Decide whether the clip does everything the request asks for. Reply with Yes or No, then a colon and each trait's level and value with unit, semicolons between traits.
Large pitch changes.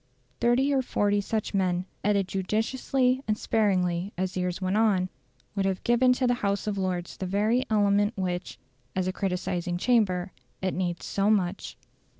No: average, 3.0 semitones